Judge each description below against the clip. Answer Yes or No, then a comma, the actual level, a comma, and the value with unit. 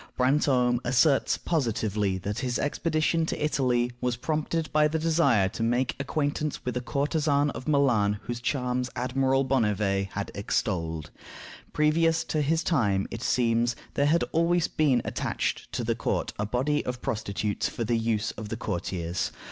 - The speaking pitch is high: No, low, 125 Hz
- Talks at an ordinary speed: Yes, average, 155 wpm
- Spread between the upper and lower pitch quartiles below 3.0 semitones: No, average, 5.3 semitones